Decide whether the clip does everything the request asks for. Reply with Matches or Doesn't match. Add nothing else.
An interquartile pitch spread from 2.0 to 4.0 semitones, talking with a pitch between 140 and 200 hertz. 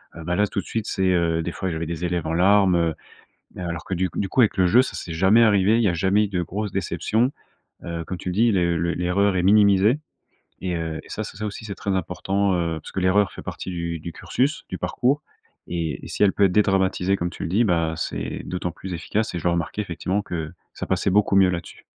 Doesn't match